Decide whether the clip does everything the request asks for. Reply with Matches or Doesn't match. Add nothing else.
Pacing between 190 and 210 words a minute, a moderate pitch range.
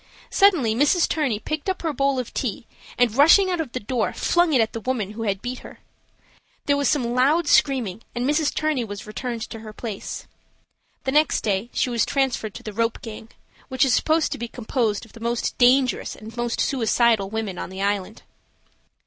Matches